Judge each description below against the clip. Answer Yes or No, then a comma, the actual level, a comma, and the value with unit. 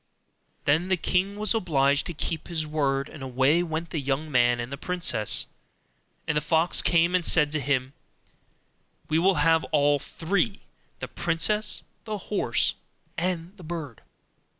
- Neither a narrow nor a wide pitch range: Yes, average, 3.7 semitones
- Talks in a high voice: No, medium, 160 Hz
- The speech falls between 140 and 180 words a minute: Yes, average, 155 wpm